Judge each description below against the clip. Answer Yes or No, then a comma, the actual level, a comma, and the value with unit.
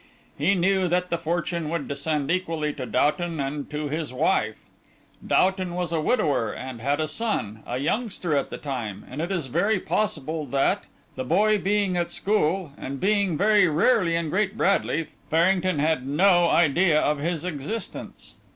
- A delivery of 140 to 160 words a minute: No, average, 170 wpm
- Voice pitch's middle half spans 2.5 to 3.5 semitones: No, average, 4.3 semitones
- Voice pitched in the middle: Yes, medium, 165 Hz